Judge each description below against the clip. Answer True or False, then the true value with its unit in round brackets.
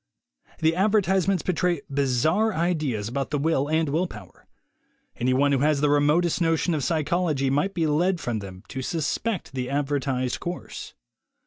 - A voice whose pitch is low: False (150 Hz)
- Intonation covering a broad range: False (4.1 semitones)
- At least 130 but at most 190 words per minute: True (155 wpm)